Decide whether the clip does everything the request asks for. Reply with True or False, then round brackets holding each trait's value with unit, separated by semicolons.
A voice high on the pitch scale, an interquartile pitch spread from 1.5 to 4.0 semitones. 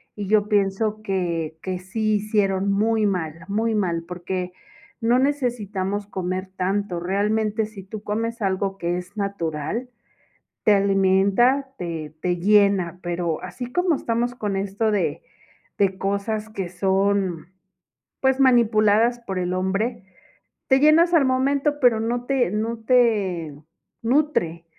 True (205 Hz; 3.6 semitones)